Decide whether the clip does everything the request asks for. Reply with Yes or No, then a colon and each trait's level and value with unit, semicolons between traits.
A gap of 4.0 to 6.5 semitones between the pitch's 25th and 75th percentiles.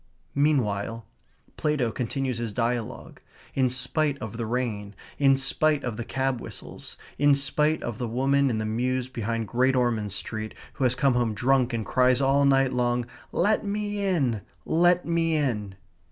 No: average, 3.3 semitones